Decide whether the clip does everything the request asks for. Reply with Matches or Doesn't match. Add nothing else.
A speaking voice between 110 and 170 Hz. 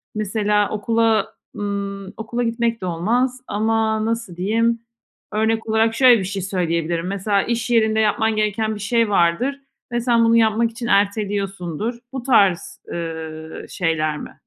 Doesn't match